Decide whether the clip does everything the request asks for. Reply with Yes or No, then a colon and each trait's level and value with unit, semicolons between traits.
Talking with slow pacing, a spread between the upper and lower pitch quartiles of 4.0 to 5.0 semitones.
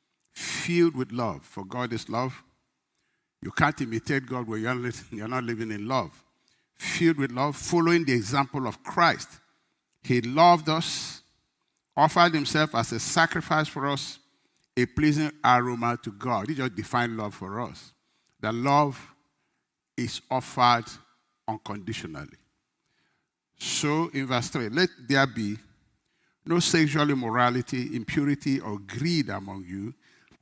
Yes: slow, 130 wpm; average, 4.5 semitones